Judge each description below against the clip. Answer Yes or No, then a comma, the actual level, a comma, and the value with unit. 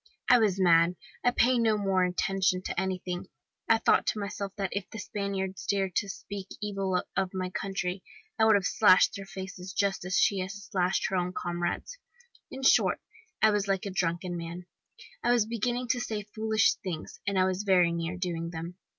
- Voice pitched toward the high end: Yes, high, 195 Hz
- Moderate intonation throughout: No, narrow, 2.3 semitones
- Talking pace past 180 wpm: Yes, average, 195 wpm